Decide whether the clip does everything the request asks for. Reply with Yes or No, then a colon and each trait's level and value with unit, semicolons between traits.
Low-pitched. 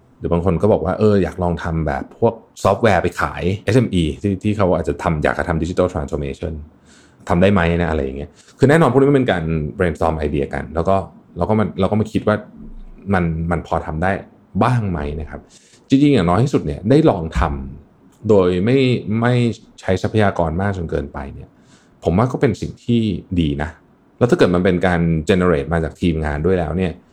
Yes: very low, 90 Hz